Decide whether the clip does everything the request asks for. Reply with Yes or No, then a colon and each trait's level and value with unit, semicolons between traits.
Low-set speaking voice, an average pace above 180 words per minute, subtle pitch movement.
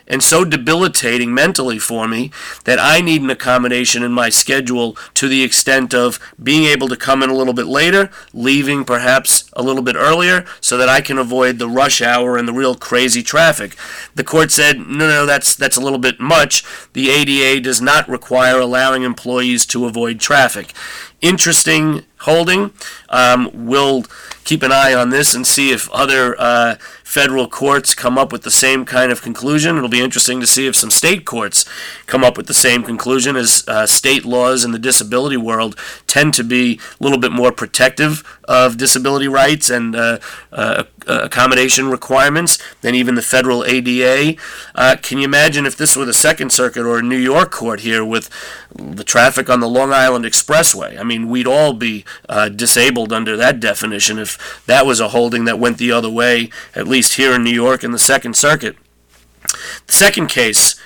Yes: low, 130 Hz; average, 190 wpm; narrow, 2.1 semitones